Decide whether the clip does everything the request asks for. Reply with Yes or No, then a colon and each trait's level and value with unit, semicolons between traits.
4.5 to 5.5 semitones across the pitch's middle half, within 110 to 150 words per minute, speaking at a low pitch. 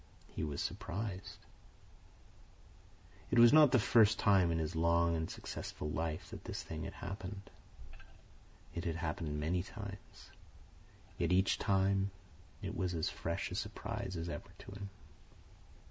No: average, 3.4 semitones; average, 145 wpm; very low, 90 Hz